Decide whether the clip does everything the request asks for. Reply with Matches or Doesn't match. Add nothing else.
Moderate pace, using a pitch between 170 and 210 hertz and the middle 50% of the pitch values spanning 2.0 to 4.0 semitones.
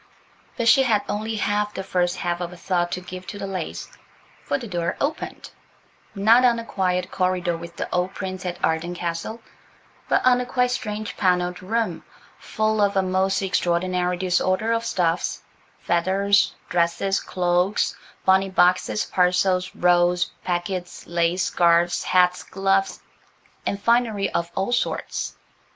Matches